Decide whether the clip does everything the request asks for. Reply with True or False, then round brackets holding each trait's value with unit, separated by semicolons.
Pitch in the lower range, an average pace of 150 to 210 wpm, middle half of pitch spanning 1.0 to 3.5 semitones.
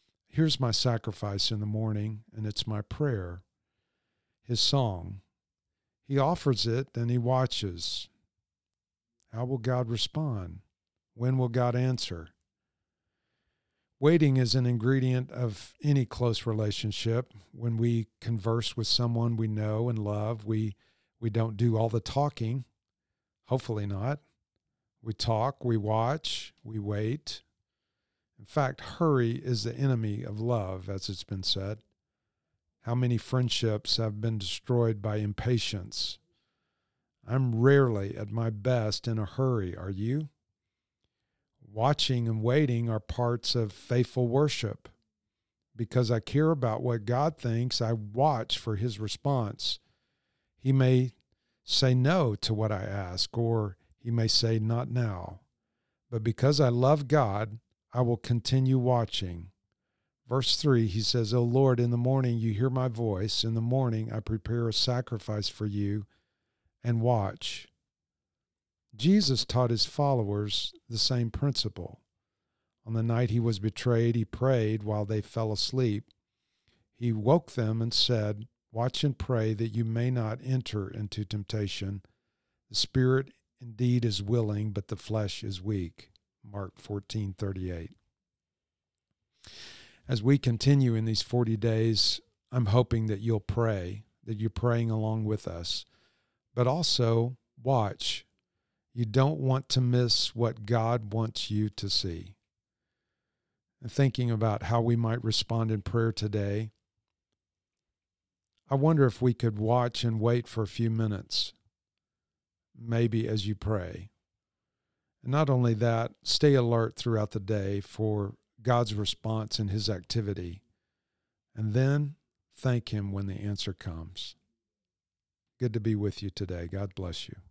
False (115 Hz; 135 wpm; 2.9 semitones)